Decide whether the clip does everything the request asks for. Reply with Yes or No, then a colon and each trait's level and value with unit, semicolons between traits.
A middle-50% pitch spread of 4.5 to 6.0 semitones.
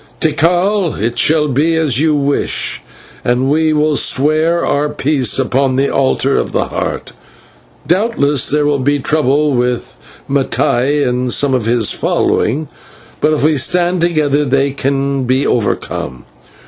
No: average, 2.9 semitones